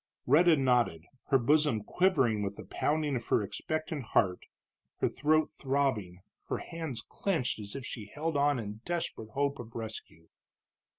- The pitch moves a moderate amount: No, wide, 5.7 semitones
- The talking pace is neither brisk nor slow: Yes, average, 155 wpm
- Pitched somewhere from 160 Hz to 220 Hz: No, low, 135 Hz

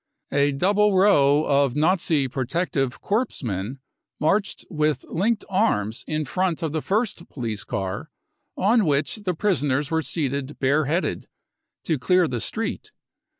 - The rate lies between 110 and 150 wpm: Yes, average, 140 wpm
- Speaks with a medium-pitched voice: Yes, medium, 155 Hz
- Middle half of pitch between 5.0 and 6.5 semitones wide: Yes, wide, 5.4 semitones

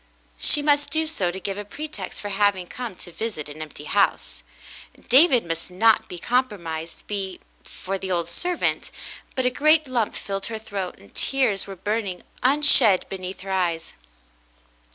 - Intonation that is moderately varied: No, wide, 5.7 semitones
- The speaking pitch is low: No, high, 200 Hz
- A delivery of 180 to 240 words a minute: No, average, 165 wpm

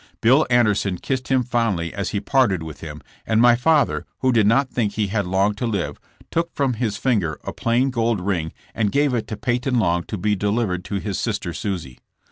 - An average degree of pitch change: Yes, average, 4.2 semitones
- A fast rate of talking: Yes, fast, 210 wpm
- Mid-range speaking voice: No, low, 110 Hz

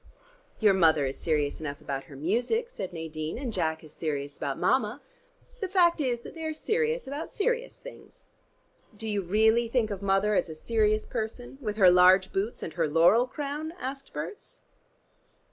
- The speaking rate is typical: Yes, average, 180 wpm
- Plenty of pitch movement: Yes, wide, 8.8 semitones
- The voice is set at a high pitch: Yes, high, 215 Hz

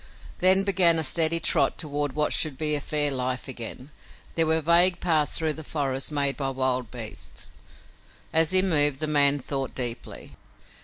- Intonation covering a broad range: No, average, 3.3 semitones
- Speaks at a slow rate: No, average, 165 wpm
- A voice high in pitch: No, medium, 145 Hz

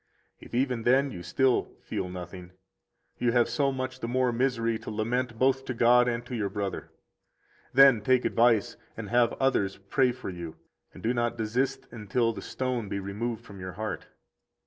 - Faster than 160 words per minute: Yes, average, 180 wpm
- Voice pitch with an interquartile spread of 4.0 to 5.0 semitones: No, average, 3.2 semitones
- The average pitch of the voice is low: Yes, low, 120 Hz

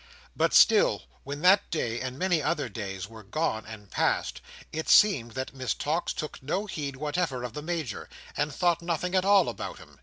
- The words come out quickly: No, average, 190 wpm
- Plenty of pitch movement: Yes, wide, 5.9 semitones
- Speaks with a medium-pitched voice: Yes, medium, 150 Hz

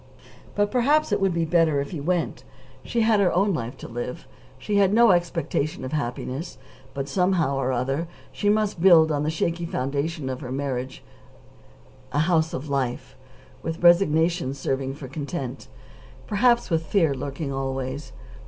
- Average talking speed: Yes, average, 160 wpm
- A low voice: No, medium, 160 Hz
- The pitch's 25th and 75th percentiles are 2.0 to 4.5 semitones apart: No, average, 4.9 semitones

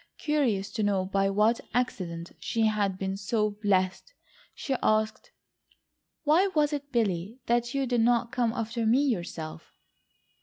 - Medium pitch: No, high, 220 Hz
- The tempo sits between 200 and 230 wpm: No, average, 145 wpm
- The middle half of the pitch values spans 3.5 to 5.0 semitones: Yes, average, 4.1 semitones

